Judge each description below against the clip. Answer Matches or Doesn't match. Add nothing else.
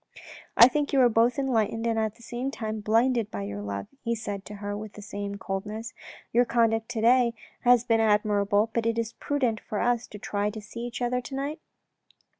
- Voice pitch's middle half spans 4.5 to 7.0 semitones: Doesn't match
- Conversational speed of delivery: Doesn't match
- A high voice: Matches